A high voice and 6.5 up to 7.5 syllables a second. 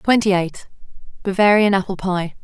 No: high, 195 Hz; 5.0 syllables/s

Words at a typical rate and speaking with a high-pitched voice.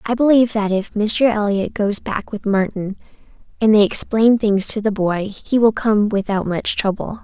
Yes: average, 190 wpm; high, 210 Hz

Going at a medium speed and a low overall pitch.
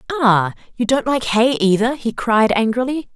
No: average, 170 wpm; high, 235 Hz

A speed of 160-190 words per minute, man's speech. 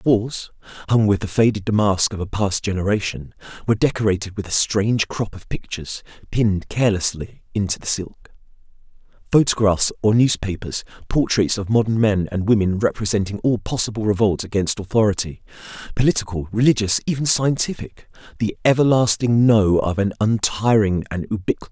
No: average, 140 wpm; male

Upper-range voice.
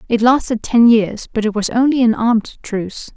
Yes: high, 230 Hz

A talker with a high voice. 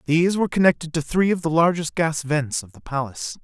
No: medium, 160 Hz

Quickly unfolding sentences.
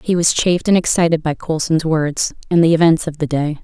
Yes: fast, 230 wpm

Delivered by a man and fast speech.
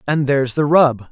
Yes: male; fast, 215 wpm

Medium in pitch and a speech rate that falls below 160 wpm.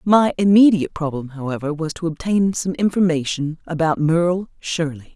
Yes: medium, 165 Hz; average, 140 wpm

